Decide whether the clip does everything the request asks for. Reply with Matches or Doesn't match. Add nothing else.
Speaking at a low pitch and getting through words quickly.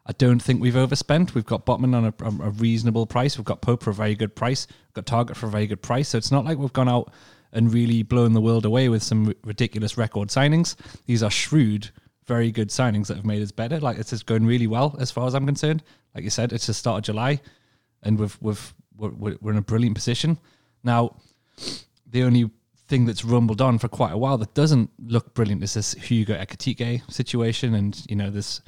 Matches